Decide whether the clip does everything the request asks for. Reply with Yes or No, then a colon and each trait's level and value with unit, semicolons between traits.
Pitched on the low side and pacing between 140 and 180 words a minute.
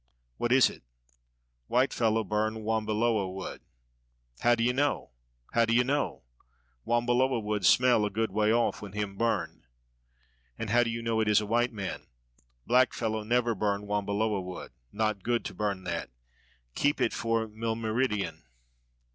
Yes: low, 110 Hz; average, 155 wpm